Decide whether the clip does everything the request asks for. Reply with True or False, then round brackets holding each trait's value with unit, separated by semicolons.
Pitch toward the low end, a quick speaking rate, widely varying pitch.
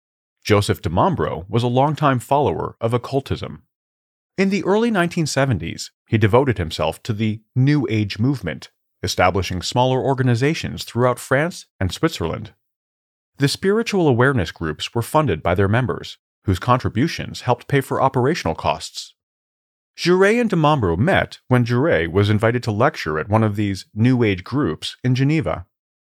False (120 Hz; 145 wpm; 6.0 semitones)